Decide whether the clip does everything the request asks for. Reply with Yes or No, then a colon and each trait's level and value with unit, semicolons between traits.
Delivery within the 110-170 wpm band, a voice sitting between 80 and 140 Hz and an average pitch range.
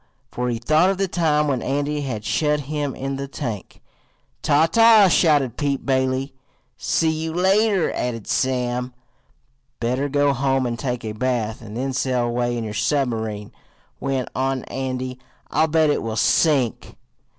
Yes: average, 160 wpm; low, 135 Hz; average, 3.4 semitones